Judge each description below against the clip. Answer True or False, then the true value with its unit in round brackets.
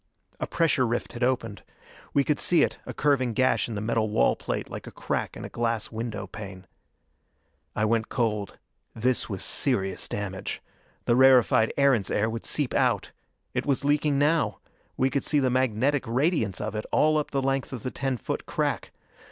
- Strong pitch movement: False (4.1 semitones)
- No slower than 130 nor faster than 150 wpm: False (185 wpm)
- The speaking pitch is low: True (120 Hz)